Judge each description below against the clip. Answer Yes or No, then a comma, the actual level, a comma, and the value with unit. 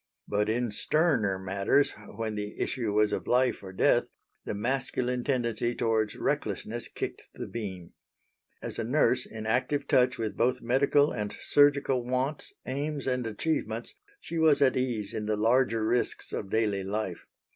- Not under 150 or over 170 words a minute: Yes, average, 155 wpm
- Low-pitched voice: Yes, low, 120 Hz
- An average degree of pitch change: Yes, average, 3.6 semitones